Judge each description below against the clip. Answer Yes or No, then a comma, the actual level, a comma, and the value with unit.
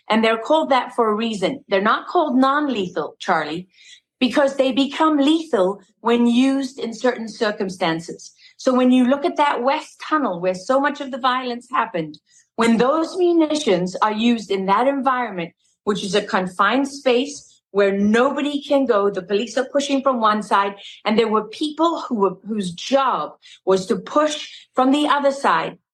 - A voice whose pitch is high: Yes, high, 245 Hz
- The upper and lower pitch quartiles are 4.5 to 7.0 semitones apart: Yes, wide, 5.5 semitones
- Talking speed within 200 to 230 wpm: No, average, 175 wpm